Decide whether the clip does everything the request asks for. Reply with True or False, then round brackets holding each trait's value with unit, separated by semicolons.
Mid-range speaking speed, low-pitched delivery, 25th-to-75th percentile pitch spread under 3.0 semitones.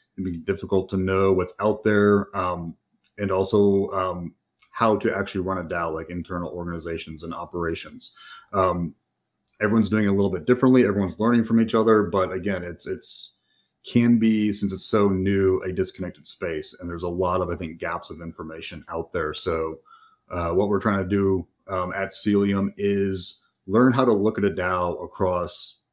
True (185 wpm; 95 Hz; 2.5 semitones)